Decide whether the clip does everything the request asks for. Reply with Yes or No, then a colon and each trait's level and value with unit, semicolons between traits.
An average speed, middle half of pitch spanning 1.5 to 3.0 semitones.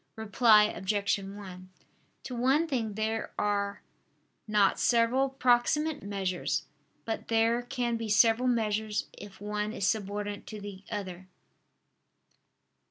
No: slow, 115 wpm; average, 2.7 semitones